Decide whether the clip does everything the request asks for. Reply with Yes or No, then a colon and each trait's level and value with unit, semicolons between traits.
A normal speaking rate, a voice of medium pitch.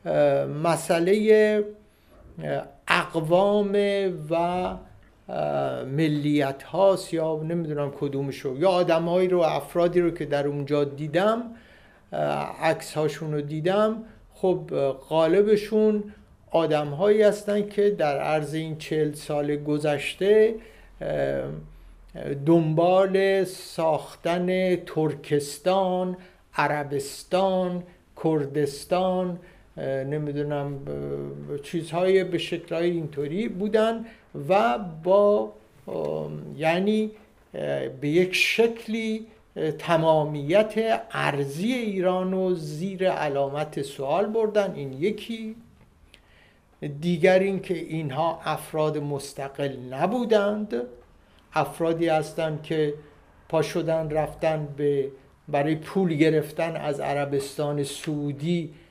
No: slow, 80 wpm; medium, 160 Hz